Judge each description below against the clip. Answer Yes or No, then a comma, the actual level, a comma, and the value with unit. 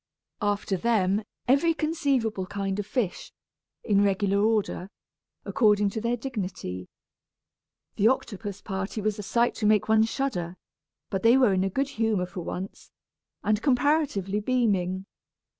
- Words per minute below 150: Yes, average, 140 wpm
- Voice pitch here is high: Yes, high, 210 Hz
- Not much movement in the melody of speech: No, average, 3.5 semitones